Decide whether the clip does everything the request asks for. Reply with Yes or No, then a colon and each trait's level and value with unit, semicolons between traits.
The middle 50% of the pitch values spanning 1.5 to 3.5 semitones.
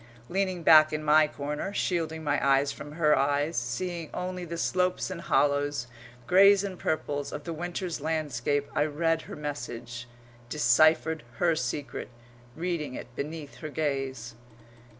Yes: average, 2.9 semitones